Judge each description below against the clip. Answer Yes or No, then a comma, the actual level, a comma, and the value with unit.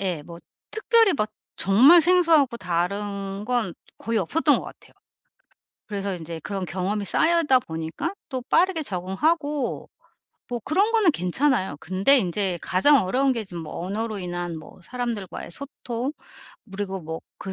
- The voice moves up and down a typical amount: No, wide, 7.3 semitones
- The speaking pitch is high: Yes, high, 205 Hz